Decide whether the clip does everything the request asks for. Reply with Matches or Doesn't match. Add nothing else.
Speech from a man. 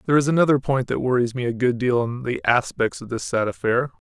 Matches